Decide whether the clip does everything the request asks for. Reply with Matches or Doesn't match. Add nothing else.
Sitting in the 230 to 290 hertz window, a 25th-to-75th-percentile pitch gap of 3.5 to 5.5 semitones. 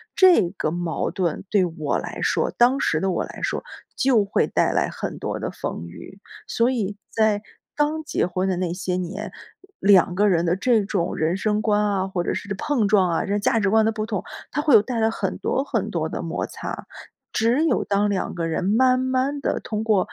Doesn't match